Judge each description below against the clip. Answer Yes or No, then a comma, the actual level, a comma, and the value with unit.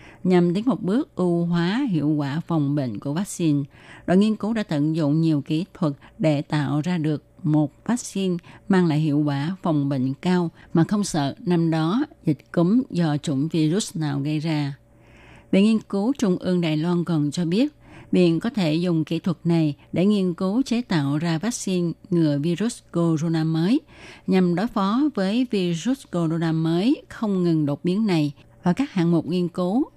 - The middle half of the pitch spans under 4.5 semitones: Yes, average, 3.9 semitones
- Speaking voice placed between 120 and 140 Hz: No, medium, 170 Hz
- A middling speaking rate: Yes, average, 185 wpm